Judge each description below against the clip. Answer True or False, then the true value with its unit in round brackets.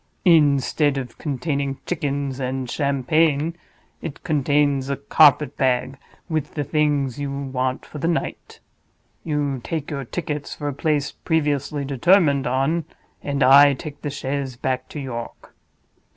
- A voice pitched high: False (140 Hz)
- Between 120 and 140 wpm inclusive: True (135 wpm)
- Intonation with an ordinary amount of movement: False (1.9 semitones)